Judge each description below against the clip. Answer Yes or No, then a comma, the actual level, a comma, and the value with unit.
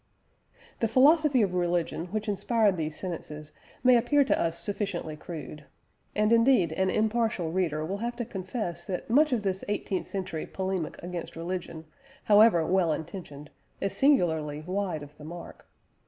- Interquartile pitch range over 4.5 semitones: Yes, average, 4.9 semitones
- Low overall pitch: No, medium, 185 Hz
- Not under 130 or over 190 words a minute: Yes, average, 155 wpm